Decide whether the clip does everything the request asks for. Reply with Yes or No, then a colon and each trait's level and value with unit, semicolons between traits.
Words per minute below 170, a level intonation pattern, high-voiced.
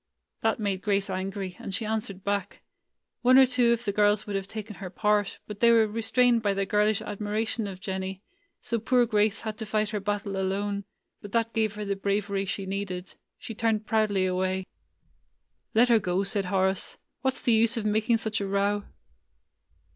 No: average, 190 wpm; narrow, 2.1 semitones; high, 205 Hz